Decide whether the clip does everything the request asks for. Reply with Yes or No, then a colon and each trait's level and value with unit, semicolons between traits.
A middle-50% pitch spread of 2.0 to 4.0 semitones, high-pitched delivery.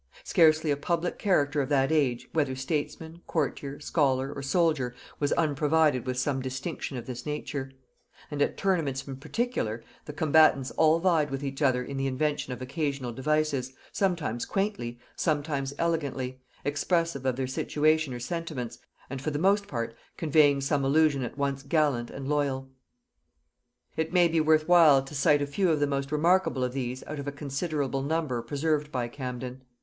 No: average, 3.0 semitones; medium, 145 Hz